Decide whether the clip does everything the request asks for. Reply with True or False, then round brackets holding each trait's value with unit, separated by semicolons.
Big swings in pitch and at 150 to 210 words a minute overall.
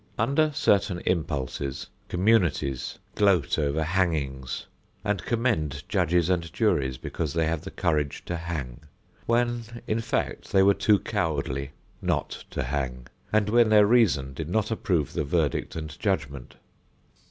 False (6.6 semitones; 140 wpm)